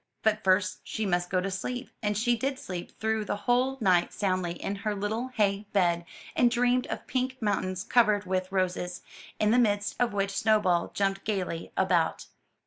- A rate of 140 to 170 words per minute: No, average, 180 wpm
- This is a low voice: No, high, 205 Hz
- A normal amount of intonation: Yes, average, 3.0 semitones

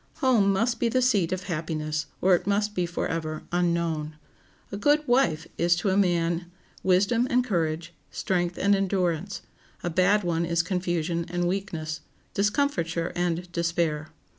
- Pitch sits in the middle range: Yes, medium, 175 Hz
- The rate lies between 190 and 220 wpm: No, average, 150 wpm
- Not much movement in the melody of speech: No, average, 3.1 semitones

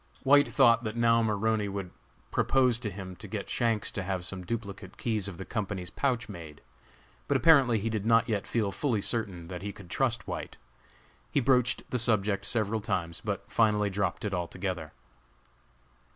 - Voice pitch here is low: Yes, low, 105 Hz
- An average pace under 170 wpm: No, average, 175 wpm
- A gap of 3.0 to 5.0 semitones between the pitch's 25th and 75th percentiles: Yes, average, 3.3 semitones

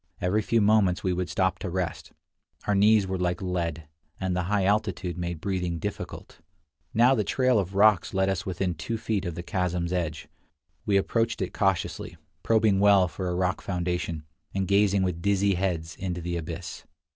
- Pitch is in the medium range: No, very low, 95 Hz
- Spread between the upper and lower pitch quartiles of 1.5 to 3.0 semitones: Yes, narrow, 2.4 semitones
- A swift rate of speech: No, average, 180 wpm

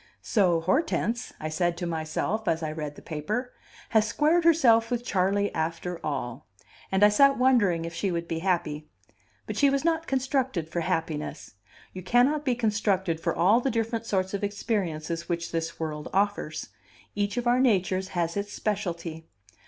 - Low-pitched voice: No, high, 190 Hz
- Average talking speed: Yes, average, 170 wpm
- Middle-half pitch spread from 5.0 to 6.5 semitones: Yes, wide, 5.6 semitones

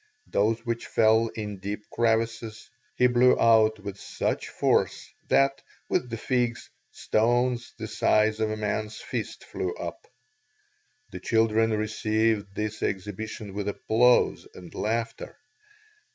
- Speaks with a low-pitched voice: Yes, low, 110 Hz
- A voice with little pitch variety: Yes, narrow, 1.6 semitones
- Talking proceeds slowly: Yes, slow, 125 wpm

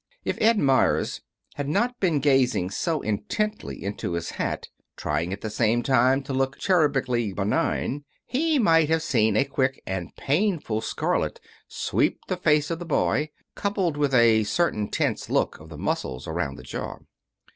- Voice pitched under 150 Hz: Yes, low, 135 Hz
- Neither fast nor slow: Yes, average, 165 wpm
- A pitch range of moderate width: No, wide, 7.2 semitones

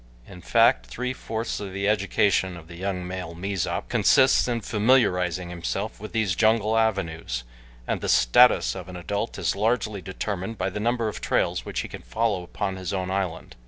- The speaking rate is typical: Yes, average, 185 wpm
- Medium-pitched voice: No, low, 100 Hz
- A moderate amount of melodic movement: Yes, average, 3.6 semitones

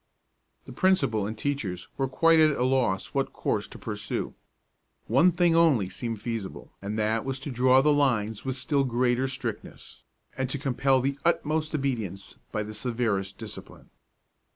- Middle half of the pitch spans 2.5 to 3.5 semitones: No, average, 4.4 semitones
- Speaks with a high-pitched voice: No, low, 130 Hz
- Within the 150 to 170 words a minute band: Yes, average, 160 wpm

